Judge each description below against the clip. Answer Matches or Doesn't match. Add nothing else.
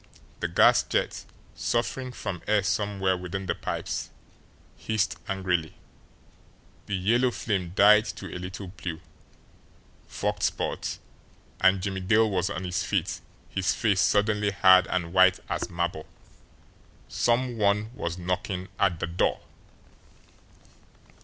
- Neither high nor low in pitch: Doesn't match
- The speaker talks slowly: Matches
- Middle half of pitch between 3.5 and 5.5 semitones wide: Doesn't match